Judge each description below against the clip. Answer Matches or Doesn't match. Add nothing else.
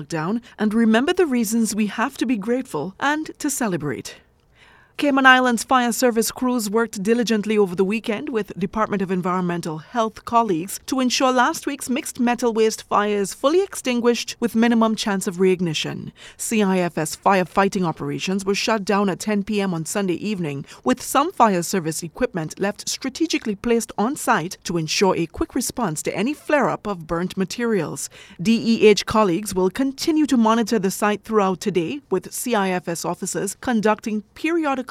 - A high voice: Matches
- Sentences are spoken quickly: Doesn't match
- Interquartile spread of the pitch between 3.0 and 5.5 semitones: Matches